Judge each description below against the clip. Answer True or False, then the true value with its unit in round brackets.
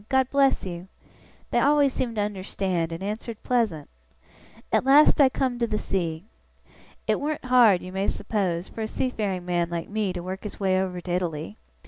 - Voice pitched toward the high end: True (200 Hz)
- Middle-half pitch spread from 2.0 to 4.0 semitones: False (5.4 semitones)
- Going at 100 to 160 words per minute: False (185 wpm)